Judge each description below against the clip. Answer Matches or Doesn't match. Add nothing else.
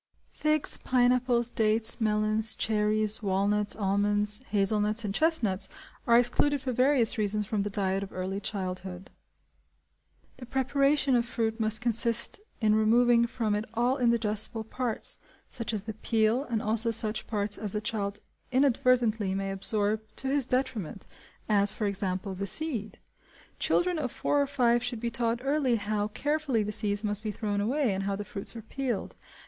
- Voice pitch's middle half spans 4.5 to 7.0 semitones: Doesn't match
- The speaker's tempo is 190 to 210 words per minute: Doesn't match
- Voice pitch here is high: Matches